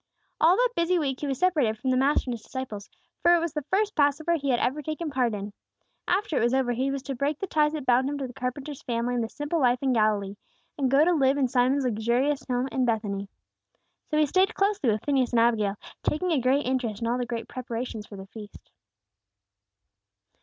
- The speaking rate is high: Yes, fast, 230 wpm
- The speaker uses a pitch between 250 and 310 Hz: Yes, very high, 260 Hz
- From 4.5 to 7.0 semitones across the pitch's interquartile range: No, average, 4.1 semitones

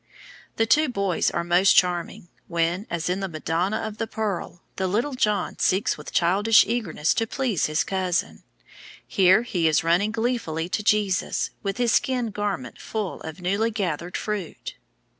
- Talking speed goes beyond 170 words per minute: No, average, 160 wpm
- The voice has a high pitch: Yes, high, 195 Hz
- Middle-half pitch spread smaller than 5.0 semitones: Yes, average, 4.2 semitones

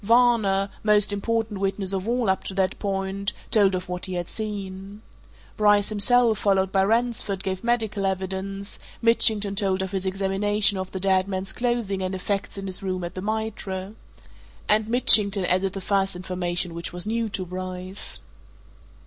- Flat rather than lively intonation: Yes, narrow, 2.0 semitones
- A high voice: Yes, high, 195 Hz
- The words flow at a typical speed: Yes, average, 165 wpm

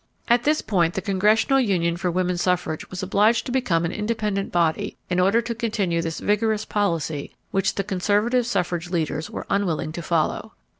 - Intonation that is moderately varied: Yes, average, 4.0 semitones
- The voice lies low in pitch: No, high, 190 Hz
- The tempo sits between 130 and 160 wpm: No, average, 180 wpm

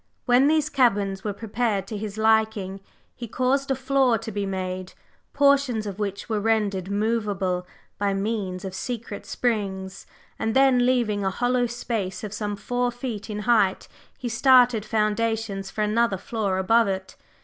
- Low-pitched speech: No, high, 215 Hz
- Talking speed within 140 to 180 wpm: Yes, average, 160 wpm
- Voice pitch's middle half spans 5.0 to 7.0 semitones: No, average, 3.6 semitones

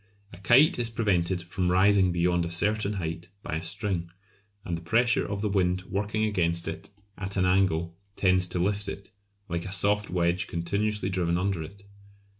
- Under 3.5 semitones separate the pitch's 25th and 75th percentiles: Yes, average, 2.9 semitones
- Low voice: Yes, very low, 95 Hz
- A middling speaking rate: Yes, average, 180 wpm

